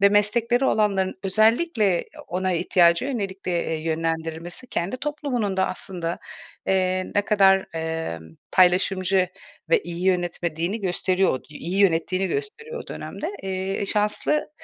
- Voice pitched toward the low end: No, high, 190 Hz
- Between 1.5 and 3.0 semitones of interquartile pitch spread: No, average, 3.4 semitones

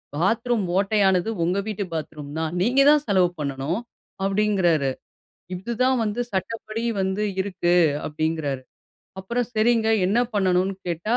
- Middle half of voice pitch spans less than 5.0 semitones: Yes, average, 4.5 semitones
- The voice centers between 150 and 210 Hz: Yes, high, 190 Hz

